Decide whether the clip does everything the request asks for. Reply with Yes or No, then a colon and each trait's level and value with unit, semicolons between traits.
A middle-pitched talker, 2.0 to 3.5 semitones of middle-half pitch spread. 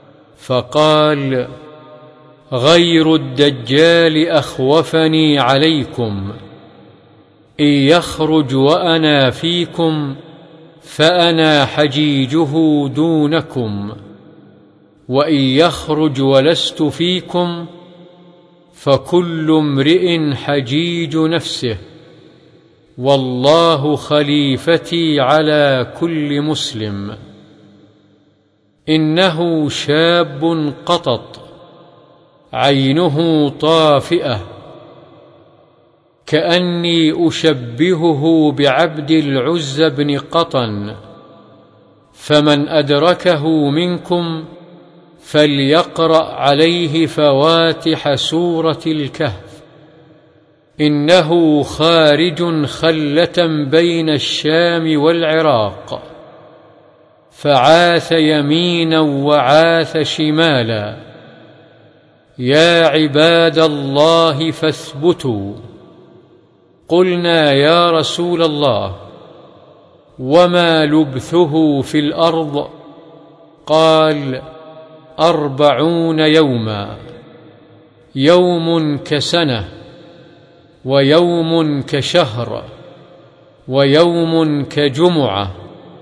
Yes: medium, 155 Hz; narrow, 2.5 semitones